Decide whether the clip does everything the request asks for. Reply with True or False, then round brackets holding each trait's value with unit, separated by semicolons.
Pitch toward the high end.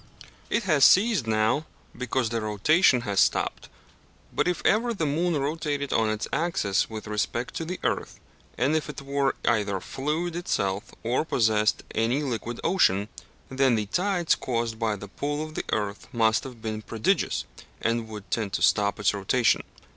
False (120 Hz)